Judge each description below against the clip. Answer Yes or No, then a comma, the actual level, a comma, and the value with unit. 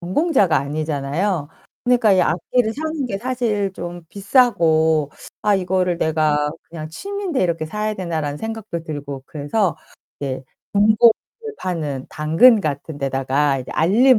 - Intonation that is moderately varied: No, wide, 6.2 semitones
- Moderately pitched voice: Yes, medium, 175 Hz